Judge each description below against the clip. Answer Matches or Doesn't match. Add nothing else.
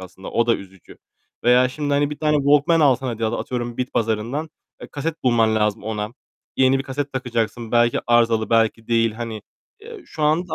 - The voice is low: Matches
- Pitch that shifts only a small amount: Doesn't match